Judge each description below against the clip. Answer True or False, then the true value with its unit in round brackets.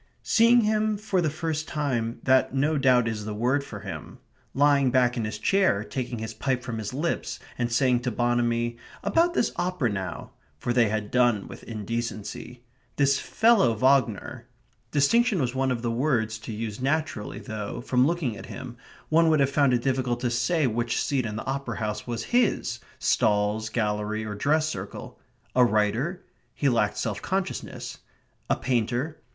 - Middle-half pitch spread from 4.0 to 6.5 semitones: True (4.4 semitones)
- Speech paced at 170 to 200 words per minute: True (175 wpm)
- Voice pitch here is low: True (125 Hz)